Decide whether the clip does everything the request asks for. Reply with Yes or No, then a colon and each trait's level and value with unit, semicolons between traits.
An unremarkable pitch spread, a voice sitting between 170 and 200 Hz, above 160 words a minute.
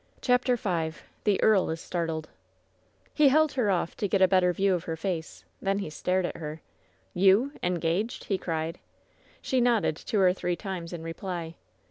Yes: average, 3.6 semitones; medium, 185 Hz; average, 175 wpm